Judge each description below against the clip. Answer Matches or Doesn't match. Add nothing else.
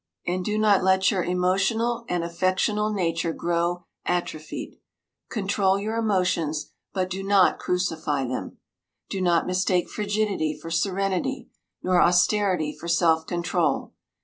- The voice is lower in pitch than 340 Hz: Matches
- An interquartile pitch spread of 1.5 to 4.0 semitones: Matches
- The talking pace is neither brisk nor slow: Doesn't match